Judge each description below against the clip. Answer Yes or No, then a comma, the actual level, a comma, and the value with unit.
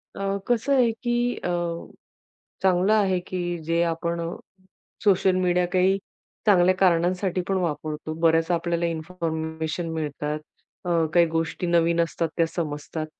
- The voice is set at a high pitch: No, medium, 175 Hz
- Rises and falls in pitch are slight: Yes, narrow, 2.2 semitones